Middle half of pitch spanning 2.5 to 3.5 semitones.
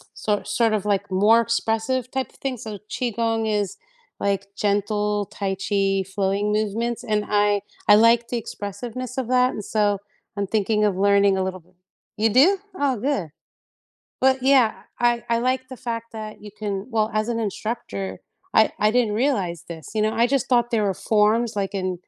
Yes: average, 2.8 semitones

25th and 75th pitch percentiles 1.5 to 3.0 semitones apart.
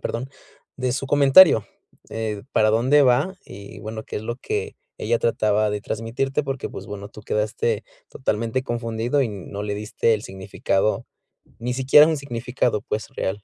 No: average, 3.6 semitones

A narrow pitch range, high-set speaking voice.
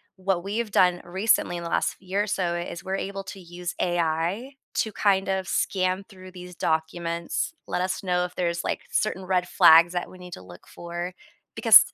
No: narrow, 1.8 semitones; medium, 180 Hz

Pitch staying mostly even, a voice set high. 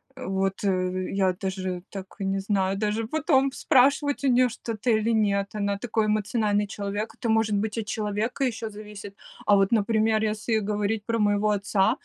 Yes: narrow, 2.0 semitones; high, 210 Hz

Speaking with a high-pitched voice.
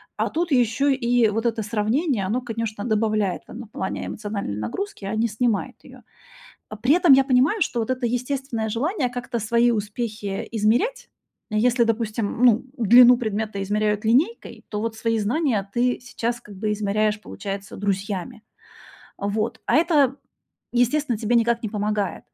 Yes: high, 230 Hz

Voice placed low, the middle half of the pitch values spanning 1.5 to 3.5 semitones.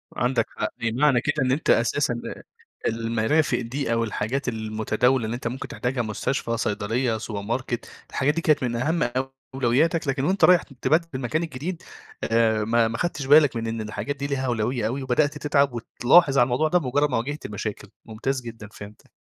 No: low, 125 Hz; average, 3.9 semitones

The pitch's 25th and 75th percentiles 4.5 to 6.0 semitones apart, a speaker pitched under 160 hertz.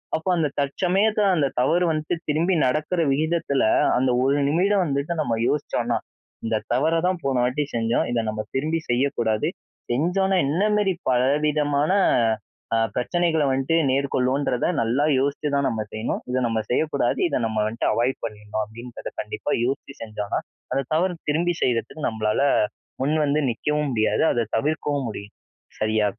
Yes: average, 5.0 semitones; medium, 140 Hz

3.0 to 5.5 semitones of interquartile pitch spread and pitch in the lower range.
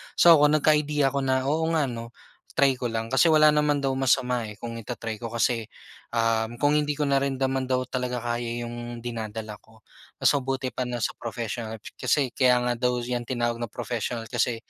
No: narrow, 2.6 semitones; low, 125 Hz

